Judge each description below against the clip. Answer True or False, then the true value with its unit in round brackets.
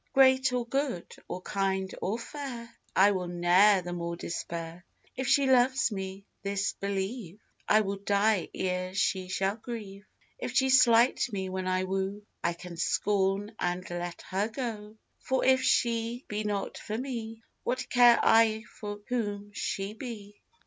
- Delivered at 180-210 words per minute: False (155 wpm)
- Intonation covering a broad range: False (3.7 semitones)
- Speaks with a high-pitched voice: True (205 Hz)